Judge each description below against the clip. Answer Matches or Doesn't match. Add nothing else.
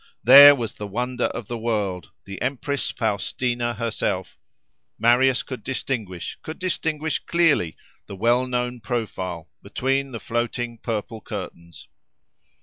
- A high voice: Doesn't match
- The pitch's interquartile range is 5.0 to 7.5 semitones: Doesn't match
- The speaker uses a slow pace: Matches